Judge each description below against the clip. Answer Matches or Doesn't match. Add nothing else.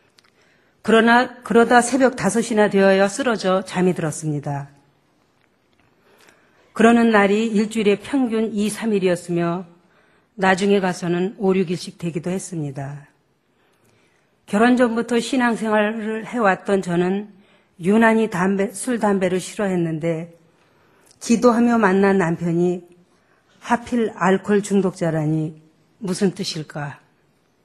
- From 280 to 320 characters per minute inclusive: Doesn't match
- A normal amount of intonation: Matches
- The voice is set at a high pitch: Matches